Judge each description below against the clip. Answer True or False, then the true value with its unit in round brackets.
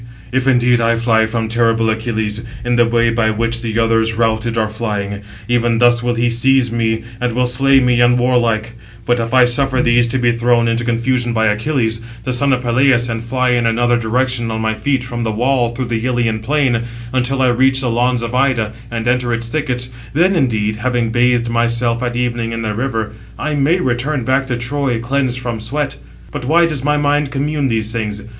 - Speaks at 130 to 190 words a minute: False (205 wpm)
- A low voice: True (120 Hz)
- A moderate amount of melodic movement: False (1.9 semitones)